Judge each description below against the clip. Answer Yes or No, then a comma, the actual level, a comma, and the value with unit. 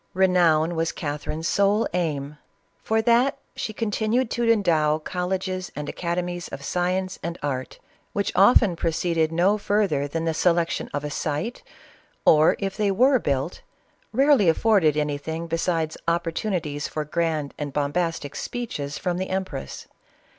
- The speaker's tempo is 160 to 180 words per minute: No, average, 145 wpm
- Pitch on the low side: No, medium, 170 Hz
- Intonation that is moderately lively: Yes, average, 4.3 semitones